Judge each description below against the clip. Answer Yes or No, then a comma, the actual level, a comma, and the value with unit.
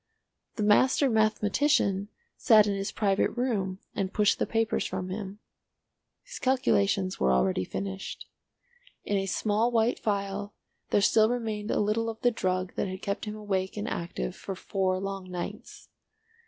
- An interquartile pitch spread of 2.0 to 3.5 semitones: Yes, narrow, 2.6 semitones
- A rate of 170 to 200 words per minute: No, average, 155 wpm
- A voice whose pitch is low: No, high, 205 Hz